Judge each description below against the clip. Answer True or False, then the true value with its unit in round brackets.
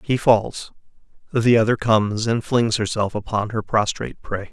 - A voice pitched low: True (110 Hz)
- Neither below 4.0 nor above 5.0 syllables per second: True (4.7 syllables/s)